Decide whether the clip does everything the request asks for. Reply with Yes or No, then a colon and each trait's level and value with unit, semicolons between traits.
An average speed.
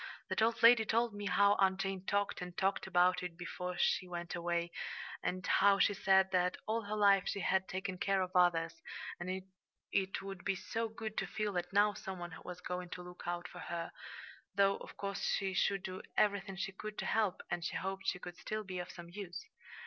No: fast, 215 wpm